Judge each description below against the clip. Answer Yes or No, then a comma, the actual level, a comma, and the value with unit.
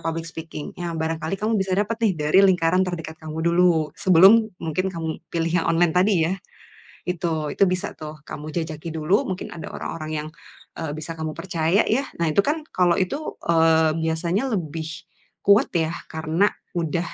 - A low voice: No, medium, 165 Hz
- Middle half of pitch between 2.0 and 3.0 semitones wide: Yes, narrow, 2.6 semitones